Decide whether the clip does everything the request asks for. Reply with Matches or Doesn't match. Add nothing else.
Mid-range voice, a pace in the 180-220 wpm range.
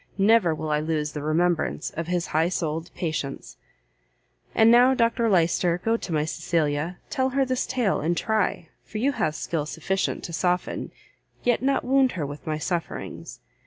Doesn't match